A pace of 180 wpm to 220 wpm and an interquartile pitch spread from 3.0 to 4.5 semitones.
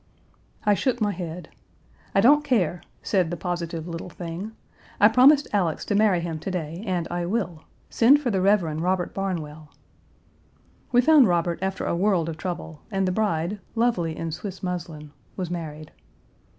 No: average, 165 wpm; average, 3.8 semitones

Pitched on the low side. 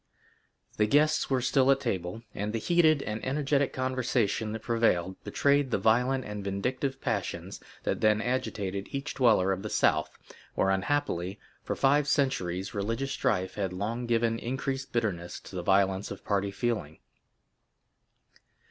Yes: low, 115 Hz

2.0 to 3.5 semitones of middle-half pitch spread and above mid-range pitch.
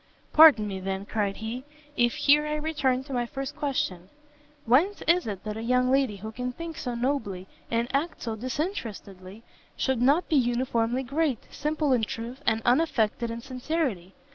No: average, 4.3 semitones; very high, 250 Hz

